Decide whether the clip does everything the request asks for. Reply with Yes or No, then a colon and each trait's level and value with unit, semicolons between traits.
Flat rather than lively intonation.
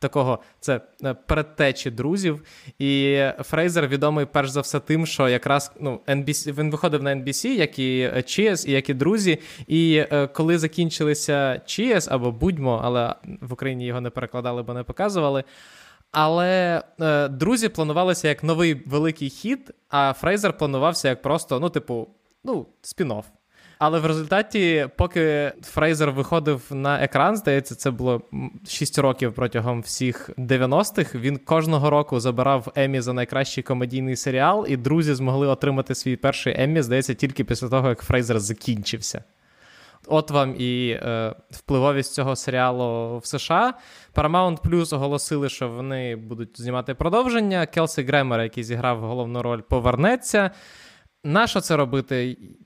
No: average, 3.8 semitones